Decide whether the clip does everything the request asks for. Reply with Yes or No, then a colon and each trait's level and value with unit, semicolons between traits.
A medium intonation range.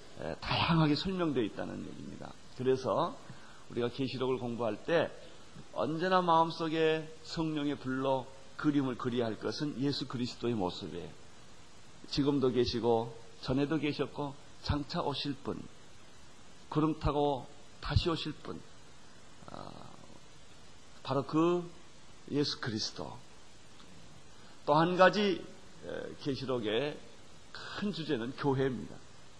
Yes: average, 4.1 semitones